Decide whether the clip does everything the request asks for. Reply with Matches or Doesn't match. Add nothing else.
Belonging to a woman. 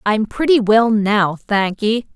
Matches